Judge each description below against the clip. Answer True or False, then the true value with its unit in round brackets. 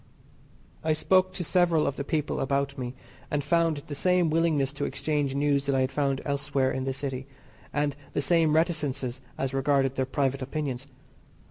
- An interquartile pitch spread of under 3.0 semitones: True (2.5 semitones)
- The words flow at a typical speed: True (175 wpm)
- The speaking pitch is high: False (140 Hz)